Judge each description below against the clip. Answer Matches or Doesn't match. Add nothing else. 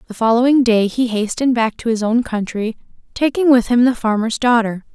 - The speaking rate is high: Doesn't match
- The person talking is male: Doesn't match